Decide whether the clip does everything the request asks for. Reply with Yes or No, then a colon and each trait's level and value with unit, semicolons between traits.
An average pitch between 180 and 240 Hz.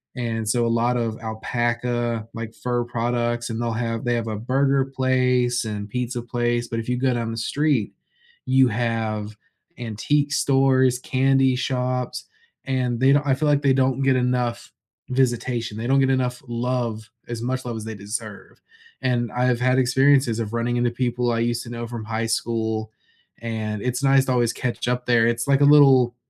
No: low, 120 Hz